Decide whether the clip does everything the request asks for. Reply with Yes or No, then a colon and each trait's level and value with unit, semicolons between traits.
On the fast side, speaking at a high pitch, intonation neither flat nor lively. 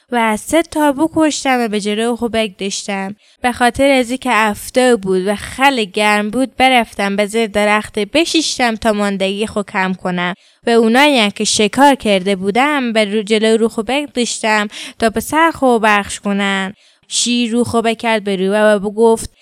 Yes: fast, 165 wpm; high, 225 Hz; average, 3.4 semitones